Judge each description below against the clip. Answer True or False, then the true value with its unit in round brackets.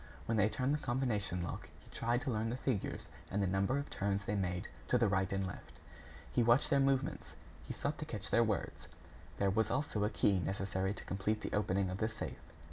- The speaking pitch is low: True (105 Hz)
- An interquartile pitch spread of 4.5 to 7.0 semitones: False (3.8 semitones)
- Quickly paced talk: True (220 wpm)